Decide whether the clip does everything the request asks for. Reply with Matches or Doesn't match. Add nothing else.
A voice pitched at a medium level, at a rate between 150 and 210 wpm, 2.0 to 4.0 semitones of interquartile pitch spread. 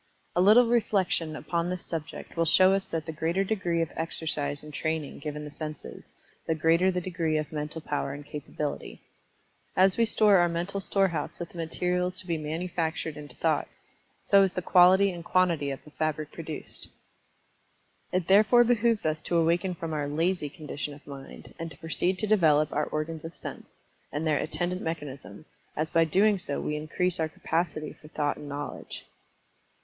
Matches